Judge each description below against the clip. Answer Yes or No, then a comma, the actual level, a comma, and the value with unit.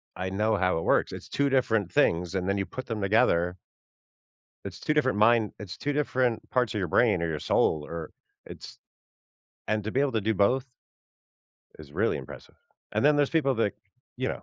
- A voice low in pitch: Yes, low, 110 Hz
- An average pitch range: No, wide, 5.8 semitones